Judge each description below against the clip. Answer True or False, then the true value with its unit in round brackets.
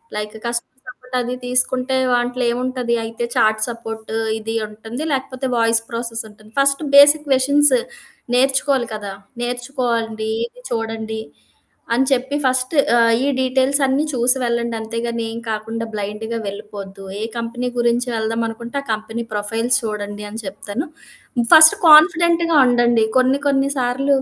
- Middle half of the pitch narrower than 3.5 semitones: True (2.8 semitones)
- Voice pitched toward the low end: False (240 Hz)